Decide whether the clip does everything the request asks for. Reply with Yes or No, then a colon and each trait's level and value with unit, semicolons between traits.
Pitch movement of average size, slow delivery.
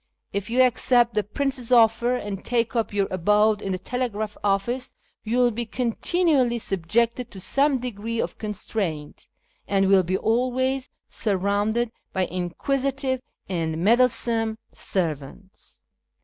Yes: average, 4.1 semitones; slow, 130 wpm